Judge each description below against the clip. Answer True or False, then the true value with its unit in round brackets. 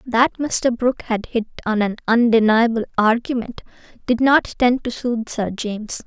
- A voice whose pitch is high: True (235 Hz)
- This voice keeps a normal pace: True (160 wpm)